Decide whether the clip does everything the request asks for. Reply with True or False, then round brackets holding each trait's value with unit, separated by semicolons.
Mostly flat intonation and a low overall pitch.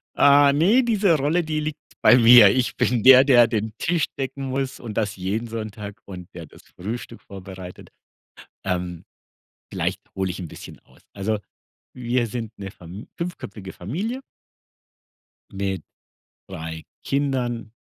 False (6.0 semitones; 115 Hz)